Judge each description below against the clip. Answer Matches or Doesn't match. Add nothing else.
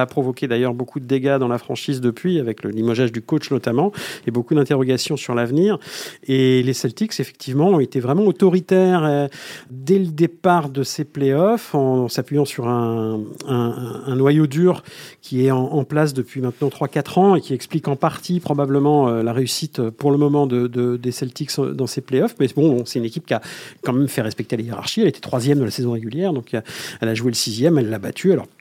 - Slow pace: Doesn't match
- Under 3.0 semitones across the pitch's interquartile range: Doesn't match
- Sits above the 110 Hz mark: Matches